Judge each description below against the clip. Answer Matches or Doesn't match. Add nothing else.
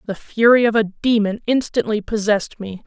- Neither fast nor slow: Matches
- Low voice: Doesn't match